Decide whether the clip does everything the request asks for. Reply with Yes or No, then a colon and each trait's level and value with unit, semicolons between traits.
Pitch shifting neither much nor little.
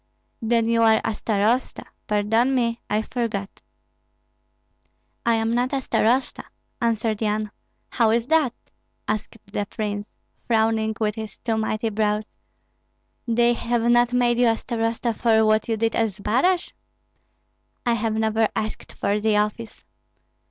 No: narrow, 1.6 semitones